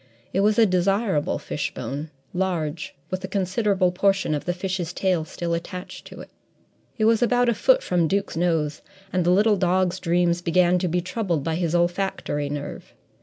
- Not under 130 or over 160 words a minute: No, average, 175 wpm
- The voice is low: No, medium, 180 Hz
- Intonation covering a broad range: No, narrow, 2.5 semitones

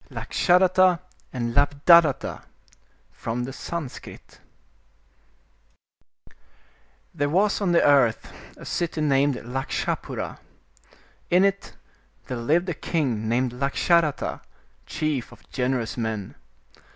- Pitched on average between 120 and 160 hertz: Yes, medium, 140 Hz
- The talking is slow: Yes, slow, 100 wpm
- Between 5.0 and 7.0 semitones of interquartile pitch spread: Yes, wide, 5.5 semitones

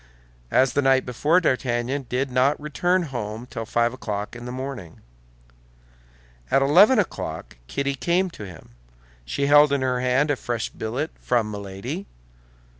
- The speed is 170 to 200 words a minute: No, average, 150 wpm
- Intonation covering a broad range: No, average, 3.6 semitones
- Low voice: Yes, low, 130 Hz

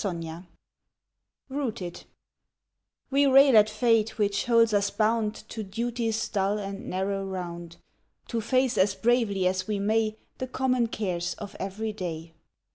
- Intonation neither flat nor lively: Yes, average, 3.3 semitones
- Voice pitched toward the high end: Yes, high, 210 Hz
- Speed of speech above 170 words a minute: No, average, 140 wpm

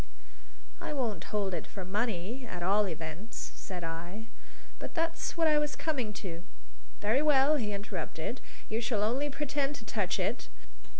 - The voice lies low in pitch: No, high, 220 Hz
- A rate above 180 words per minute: No, average, 160 wpm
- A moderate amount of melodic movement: No, wide, 6.7 semitones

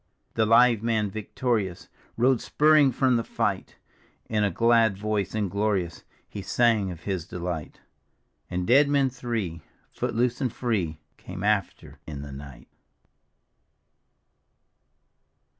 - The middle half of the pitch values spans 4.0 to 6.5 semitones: Yes, average, 4.6 semitones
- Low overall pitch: Yes, low, 105 Hz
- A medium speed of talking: No, slow, 125 wpm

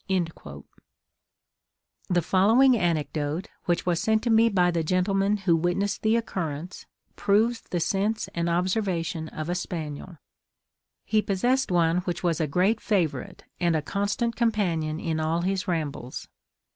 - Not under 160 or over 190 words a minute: No, average, 140 wpm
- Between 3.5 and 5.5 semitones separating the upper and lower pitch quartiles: Yes, average, 3.8 semitones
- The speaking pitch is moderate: Yes, medium, 180 Hz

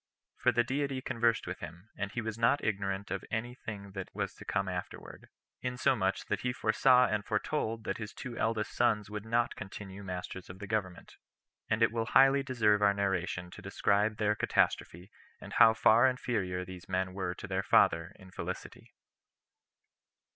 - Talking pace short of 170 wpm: No, average, 175 wpm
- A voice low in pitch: Yes, low, 105 Hz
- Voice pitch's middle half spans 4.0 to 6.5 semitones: No, average, 3.3 semitones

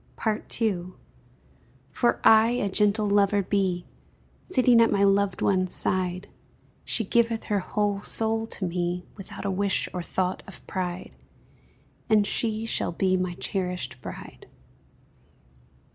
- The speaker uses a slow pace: Yes, slow, 130 wpm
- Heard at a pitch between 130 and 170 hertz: No, high, 200 Hz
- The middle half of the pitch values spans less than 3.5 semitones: Yes, average, 3.0 semitones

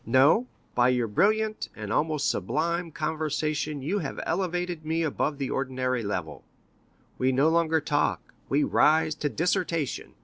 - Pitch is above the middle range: No, medium, 155 Hz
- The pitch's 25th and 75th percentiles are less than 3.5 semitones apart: No, average, 3.9 semitones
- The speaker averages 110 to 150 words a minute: Yes, average, 140 wpm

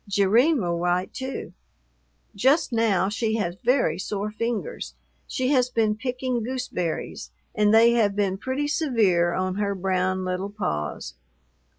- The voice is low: No, high, 210 Hz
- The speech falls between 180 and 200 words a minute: No, slow, 135 wpm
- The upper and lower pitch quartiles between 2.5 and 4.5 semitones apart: No, average, 4.9 semitones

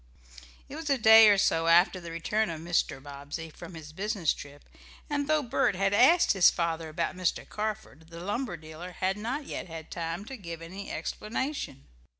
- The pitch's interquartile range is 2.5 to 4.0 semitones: No, average, 4.9 semitones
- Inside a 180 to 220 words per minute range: Yes, average, 185 wpm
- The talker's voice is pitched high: No, medium, 180 Hz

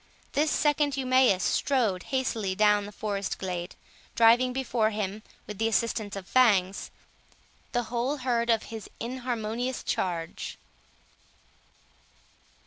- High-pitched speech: Yes, high, 225 Hz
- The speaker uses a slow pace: Yes, slow, 115 wpm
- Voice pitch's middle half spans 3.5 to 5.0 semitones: Yes, average, 3.9 semitones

